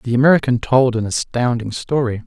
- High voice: No, low, 120 Hz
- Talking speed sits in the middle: Yes, average, 160 wpm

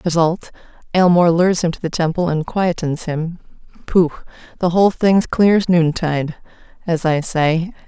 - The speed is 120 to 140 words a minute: Yes, slow, 135 wpm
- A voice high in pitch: No, medium, 170 Hz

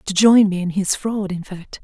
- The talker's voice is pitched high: Yes, high, 195 Hz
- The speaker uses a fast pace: Yes, fast, 260 wpm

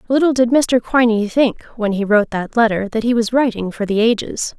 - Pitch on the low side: No, high, 225 Hz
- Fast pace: Yes, fast, 220 wpm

